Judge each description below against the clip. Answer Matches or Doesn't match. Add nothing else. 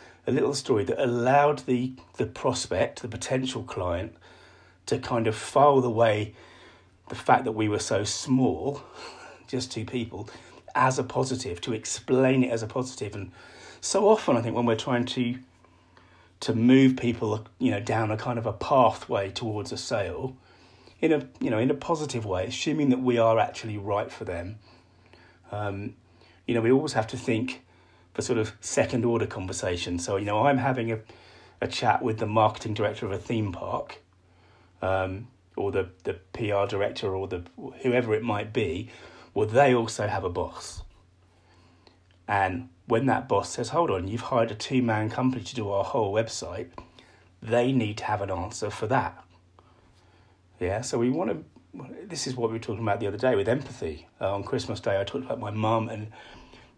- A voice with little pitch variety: Doesn't match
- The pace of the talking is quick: Doesn't match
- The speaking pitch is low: Matches